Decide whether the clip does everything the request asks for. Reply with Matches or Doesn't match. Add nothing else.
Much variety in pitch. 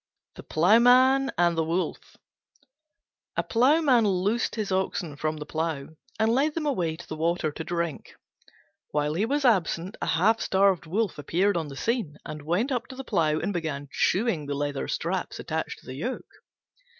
Matches